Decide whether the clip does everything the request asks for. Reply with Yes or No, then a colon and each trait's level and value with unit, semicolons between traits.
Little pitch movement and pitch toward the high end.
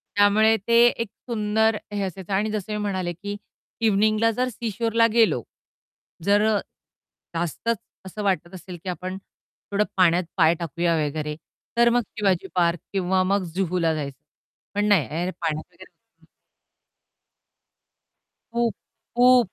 No: average, 3.7 semitones; high, 200 Hz